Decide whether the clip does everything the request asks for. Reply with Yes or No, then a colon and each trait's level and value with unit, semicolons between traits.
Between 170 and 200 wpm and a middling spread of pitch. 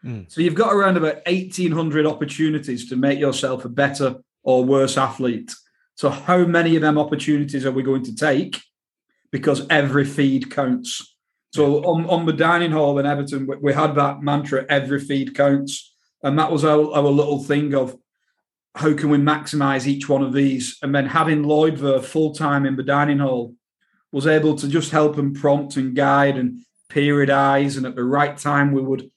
No: average, 185 wpm; narrow, 1.9 semitones